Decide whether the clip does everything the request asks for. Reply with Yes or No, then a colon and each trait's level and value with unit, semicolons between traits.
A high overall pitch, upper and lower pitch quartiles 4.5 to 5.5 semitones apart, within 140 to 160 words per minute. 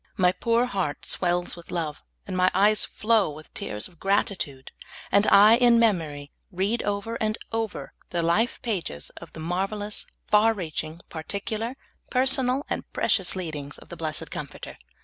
Yes: high, 195 Hz; average, 5.0 semitones; average, 155 wpm